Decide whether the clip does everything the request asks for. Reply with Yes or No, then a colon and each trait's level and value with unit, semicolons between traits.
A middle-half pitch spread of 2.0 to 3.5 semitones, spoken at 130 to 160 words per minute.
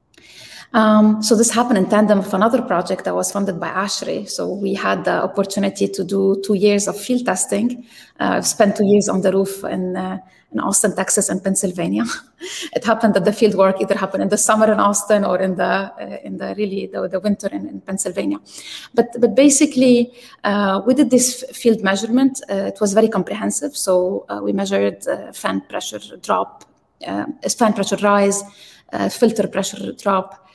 No: average, 2.9 semitones; average, 195 wpm